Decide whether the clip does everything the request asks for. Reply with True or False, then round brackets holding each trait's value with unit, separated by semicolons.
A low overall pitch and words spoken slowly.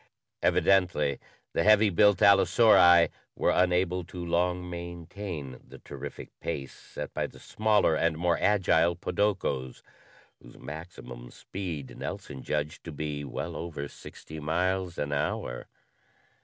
True (85 Hz; 125 wpm)